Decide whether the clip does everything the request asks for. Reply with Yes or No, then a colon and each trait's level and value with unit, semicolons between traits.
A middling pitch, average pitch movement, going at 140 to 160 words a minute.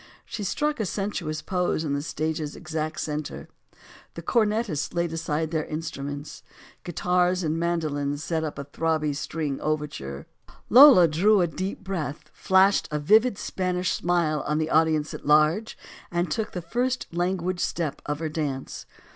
Yes: medium, 160 Hz; average, 3.2 semitones; average, 155 wpm